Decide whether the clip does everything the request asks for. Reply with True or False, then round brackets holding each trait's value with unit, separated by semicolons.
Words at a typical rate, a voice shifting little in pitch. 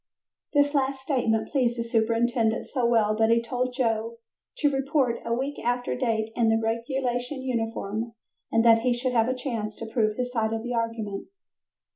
True (180 wpm; 2.1 semitones)